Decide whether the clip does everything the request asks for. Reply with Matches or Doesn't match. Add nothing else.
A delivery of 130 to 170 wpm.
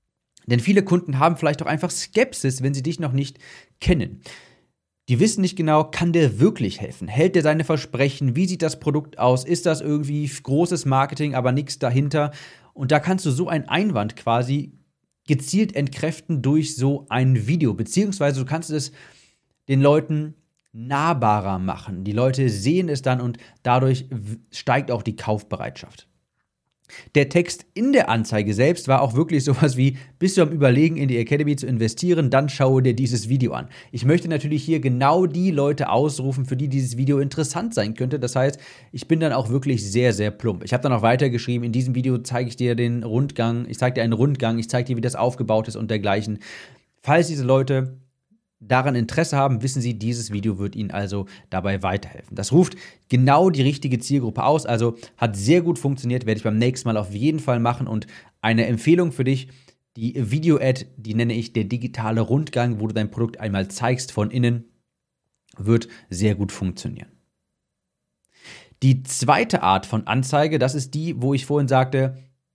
Doesn't match